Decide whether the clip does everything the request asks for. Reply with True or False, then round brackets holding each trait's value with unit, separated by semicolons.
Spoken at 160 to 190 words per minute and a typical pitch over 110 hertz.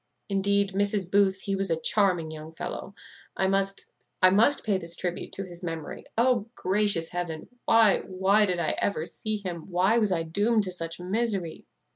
True (180 wpm; 190 Hz)